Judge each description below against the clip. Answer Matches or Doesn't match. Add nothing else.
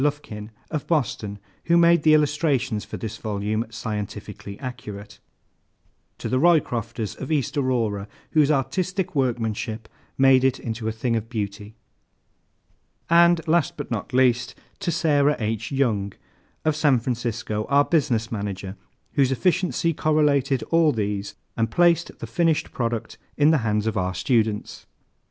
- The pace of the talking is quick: Doesn't match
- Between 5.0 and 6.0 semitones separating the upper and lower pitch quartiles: Matches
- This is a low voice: Matches